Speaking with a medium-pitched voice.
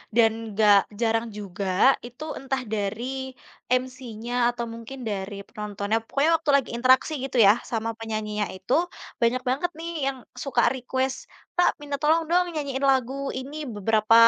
No: high, 240 Hz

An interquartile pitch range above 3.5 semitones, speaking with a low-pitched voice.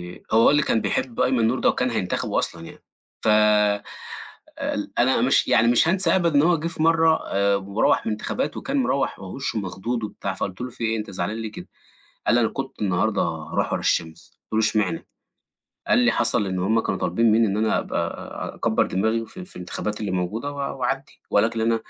Yes: average, 5.1 semitones; low, 115 Hz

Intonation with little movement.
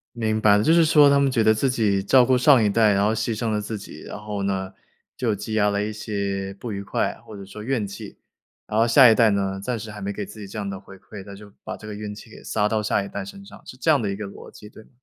Yes: narrow, 2.3 semitones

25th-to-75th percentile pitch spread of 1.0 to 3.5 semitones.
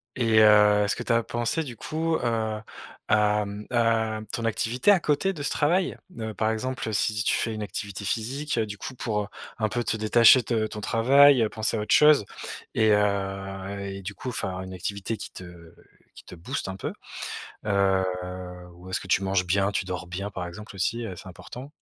Yes: average, 3.2 semitones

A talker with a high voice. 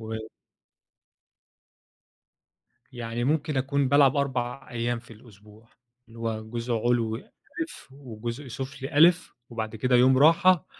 No: low, 125 Hz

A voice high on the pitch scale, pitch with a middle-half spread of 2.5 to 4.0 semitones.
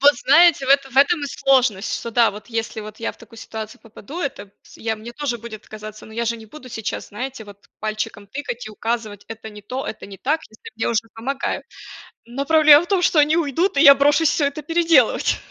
No: high, 240 Hz; average, 4.8 semitones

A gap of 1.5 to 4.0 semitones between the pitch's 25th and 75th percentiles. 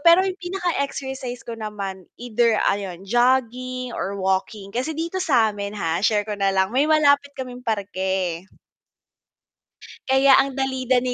No: average, 5.0 semitones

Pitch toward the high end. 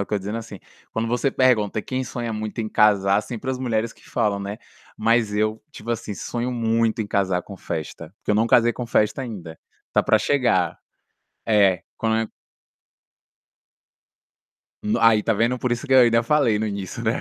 No: low, 110 Hz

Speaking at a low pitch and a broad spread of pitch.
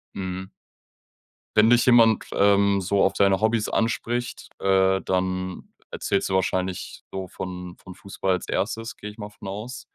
No: low, 100 Hz; narrow, 2.5 semitones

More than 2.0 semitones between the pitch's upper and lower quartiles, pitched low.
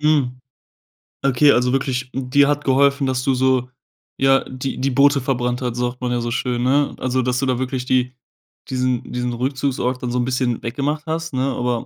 No: narrow, 1.7 semitones; low, 130 Hz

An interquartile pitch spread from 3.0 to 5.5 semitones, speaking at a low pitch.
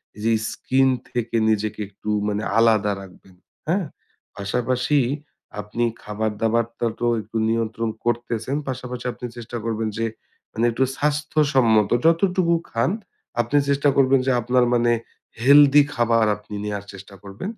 Yes: average, 3.6 semitones; low, 115 Hz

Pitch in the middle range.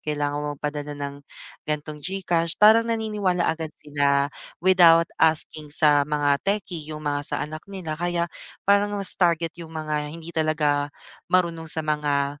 Yes: medium, 155 Hz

